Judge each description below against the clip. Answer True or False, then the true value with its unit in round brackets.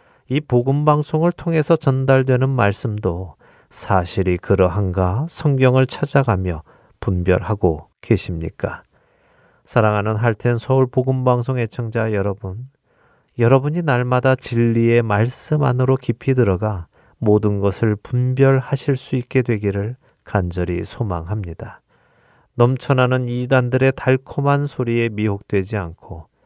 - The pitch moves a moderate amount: True (4.6 semitones)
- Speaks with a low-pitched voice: True (120 Hz)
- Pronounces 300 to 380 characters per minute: False (270 characters per minute)